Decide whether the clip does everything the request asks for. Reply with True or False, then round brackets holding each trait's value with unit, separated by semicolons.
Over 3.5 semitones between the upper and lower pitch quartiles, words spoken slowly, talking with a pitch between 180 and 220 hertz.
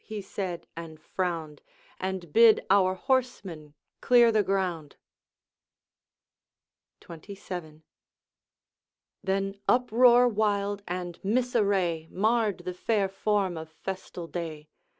True (3.9 semitones; 95 wpm; 190 Hz)